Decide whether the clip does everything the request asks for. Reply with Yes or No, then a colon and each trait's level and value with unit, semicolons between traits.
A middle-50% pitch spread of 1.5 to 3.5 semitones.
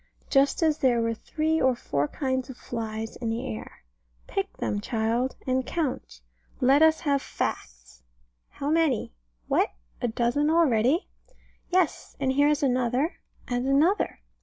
No: average, 4.3 semitones